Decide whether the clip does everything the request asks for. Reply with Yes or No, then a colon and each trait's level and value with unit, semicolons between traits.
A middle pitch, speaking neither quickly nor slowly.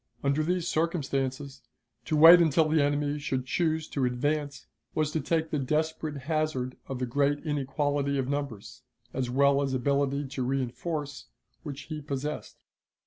Yes: medium, 145 Hz; average, 150 wpm